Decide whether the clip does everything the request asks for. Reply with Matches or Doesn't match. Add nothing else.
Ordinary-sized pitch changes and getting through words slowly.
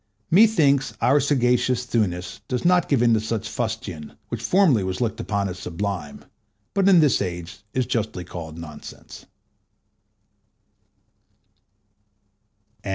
Doesn't match